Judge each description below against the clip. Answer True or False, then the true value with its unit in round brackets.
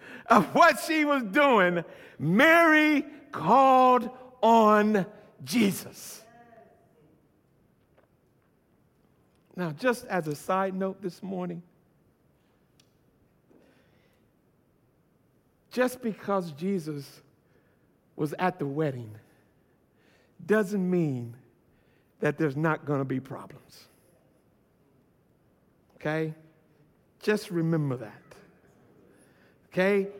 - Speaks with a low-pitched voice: False (185 Hz)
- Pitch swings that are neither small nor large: False (6.4 semitones)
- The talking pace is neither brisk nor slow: False (75 wpm)